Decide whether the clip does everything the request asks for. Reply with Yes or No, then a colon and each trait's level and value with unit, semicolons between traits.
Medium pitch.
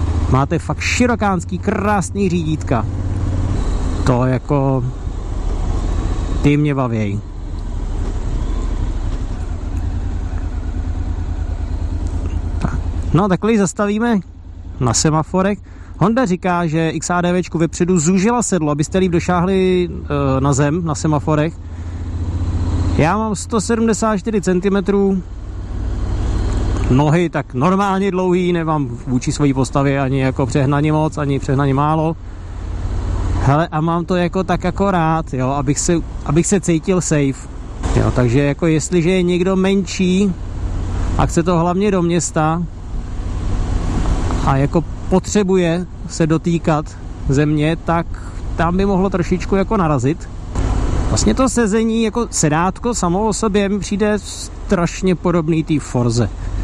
Yes: medium, 145 Hz